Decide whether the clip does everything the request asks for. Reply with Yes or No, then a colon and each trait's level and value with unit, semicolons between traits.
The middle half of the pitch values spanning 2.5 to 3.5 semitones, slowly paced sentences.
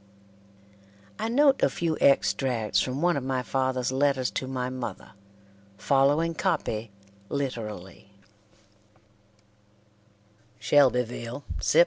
Yes: average, 2.8 semitones; slow, 95 wpm